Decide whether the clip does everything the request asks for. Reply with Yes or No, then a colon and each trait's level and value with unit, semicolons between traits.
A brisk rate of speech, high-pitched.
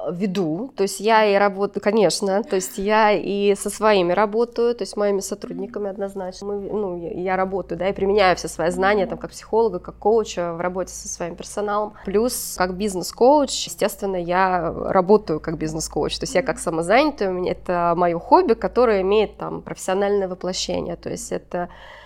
Yes: fast, 175 wpm; high, 195 Hz